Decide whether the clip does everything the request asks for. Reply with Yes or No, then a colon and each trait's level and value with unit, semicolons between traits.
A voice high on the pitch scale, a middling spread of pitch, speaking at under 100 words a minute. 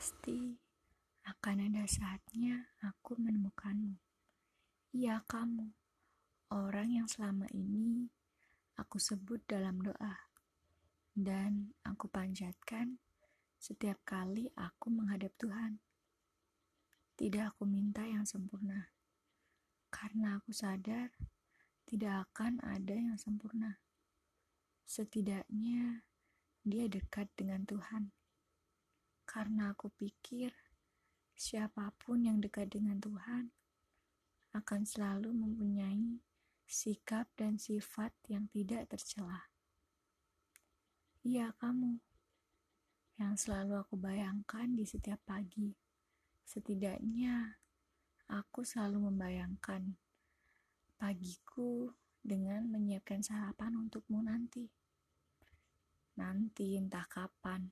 No: high, 210 Hz; narrow, 2.2 semitones; slow, 85 wpm